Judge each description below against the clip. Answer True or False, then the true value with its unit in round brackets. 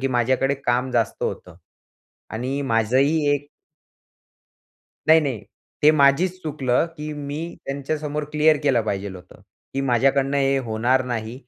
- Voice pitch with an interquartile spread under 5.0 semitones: True (3.2 semitones)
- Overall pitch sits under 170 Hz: True (135 Hz)